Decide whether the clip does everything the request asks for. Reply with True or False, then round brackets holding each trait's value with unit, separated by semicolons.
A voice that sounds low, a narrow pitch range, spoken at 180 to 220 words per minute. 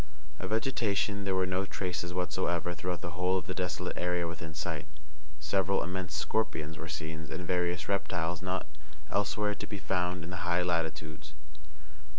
False (90 Hz; 2.2 semitones; 165 wpm)